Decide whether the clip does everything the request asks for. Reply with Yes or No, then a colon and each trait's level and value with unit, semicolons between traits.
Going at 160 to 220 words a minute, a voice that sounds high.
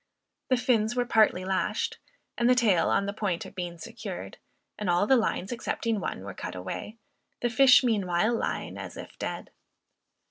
Yes: average, 175 wpm; high, 215 Hz